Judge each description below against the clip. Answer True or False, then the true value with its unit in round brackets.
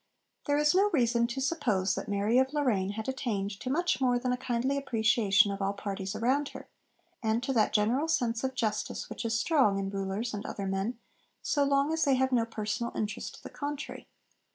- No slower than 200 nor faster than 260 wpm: True (205 wpm)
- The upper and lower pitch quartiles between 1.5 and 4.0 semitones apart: False (4.5 semitones)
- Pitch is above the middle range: True (235 Hz)